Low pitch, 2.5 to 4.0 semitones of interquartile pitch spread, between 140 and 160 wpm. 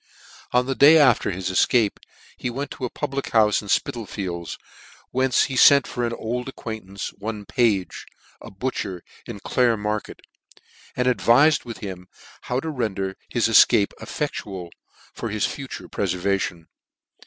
No: low, 115 Hz; average, 4.4 semitones; average, 145 wpm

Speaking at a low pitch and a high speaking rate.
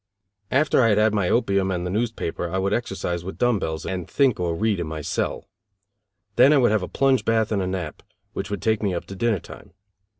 Yes: low, 100 Hz; fast, 235 wpm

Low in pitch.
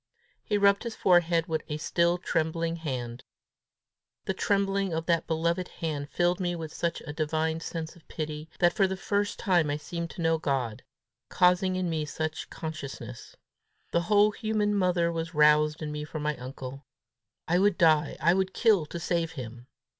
No: medium, 165 Hz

